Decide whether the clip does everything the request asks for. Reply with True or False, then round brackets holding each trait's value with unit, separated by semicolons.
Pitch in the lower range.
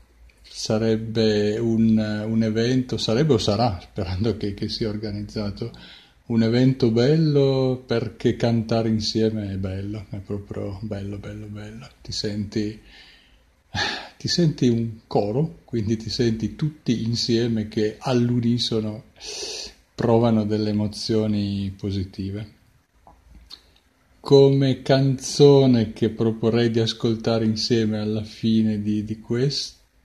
True (110 Hz)